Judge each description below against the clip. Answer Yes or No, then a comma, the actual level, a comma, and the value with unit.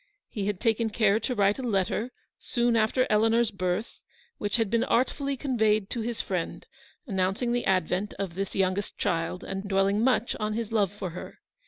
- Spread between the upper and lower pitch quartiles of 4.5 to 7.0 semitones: No, average, 3.1 semitones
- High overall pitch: Yes, high, 210 Hz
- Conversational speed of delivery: Yes, average, 180 wpm